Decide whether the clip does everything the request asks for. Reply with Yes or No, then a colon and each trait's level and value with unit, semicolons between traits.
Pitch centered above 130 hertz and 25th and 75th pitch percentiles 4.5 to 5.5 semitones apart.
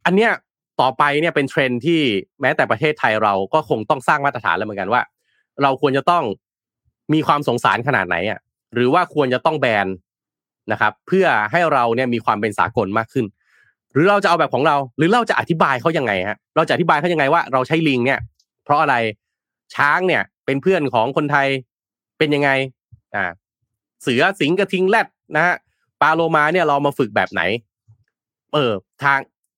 Yes: medium, 140 Hz; average, 5.2 semitones